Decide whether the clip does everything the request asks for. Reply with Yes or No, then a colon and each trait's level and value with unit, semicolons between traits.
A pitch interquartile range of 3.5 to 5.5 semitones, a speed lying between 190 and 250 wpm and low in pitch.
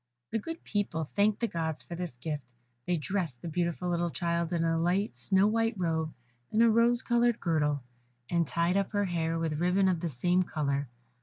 No: average, 3.8 semitones; average, 200 wpm; medium, 170 Hz